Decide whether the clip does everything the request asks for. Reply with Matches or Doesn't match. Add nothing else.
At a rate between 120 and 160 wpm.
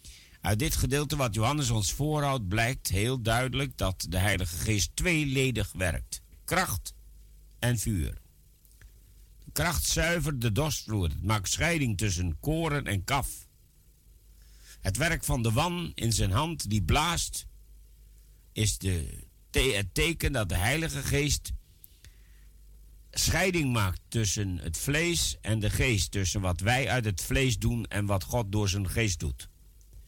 Matches